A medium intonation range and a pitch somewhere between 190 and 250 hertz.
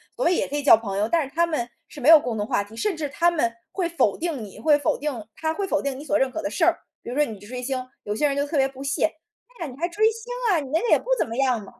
No: average, 4.8 semitones; very high, 290 Hz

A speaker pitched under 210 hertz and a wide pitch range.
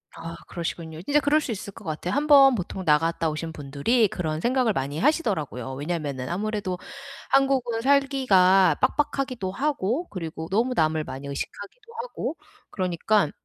Yes: high, 190 Hz; wide, 8.4 semitones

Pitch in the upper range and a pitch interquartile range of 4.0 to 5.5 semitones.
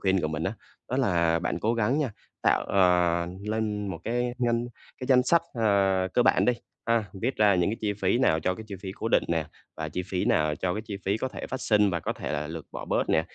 No: low, 100 Hz; average, 5.0 semitones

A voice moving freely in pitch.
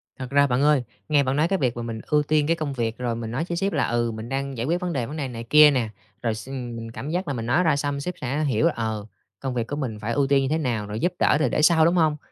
No: average, 4.4 semitones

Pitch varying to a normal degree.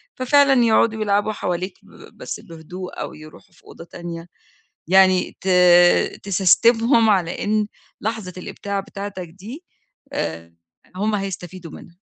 Yes: average, 3.7 semitones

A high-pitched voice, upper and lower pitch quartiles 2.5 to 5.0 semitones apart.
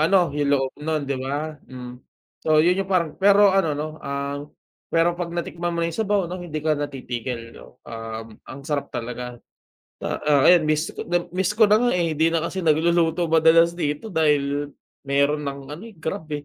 No: medium, 155 Hz; average, 3.5 semitones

